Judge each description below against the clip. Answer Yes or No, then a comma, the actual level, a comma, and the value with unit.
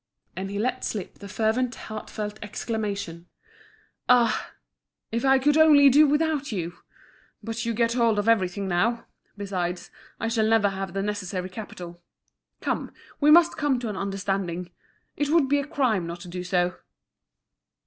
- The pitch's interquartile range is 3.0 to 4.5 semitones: No, average, 4.9 semitones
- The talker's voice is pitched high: Yes, high, 215 Hz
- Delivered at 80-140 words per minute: No, average, 160 wpm